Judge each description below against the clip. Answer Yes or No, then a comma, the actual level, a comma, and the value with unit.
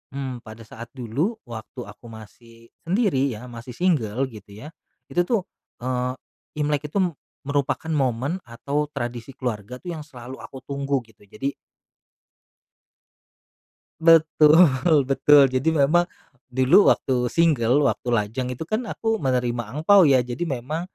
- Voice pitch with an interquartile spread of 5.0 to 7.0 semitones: No, average, 4.3 semitones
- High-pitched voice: No, low, 135 Hz